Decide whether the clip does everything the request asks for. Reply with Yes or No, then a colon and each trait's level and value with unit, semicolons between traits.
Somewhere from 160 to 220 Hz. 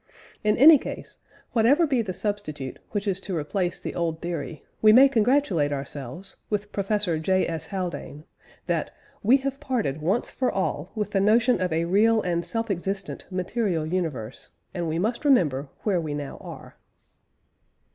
Yes: high, 190 Hz